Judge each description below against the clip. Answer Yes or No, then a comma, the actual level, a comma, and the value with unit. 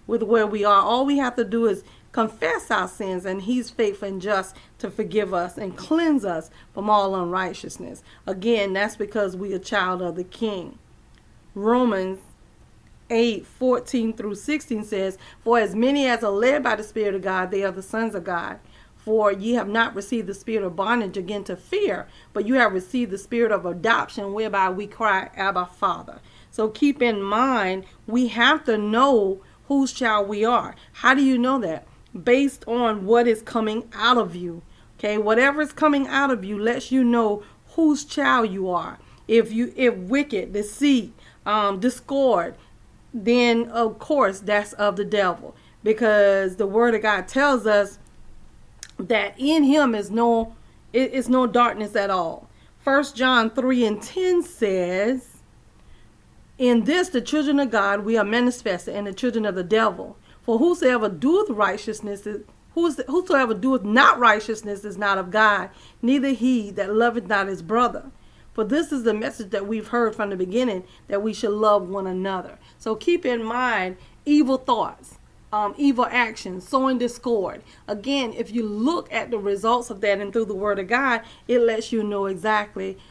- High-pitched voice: Yes, high, 225 Hz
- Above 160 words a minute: Yes, average, 175 wpm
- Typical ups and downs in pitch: Yes, average, 3.5 semitones